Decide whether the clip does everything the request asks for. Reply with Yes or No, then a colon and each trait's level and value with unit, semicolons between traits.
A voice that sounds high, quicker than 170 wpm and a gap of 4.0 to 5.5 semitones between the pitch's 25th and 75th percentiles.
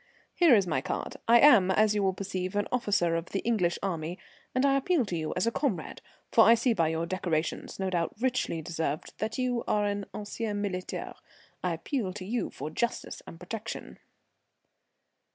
Yes: high, 200 Hz; average, 190 wpm; average, 4.9 semitones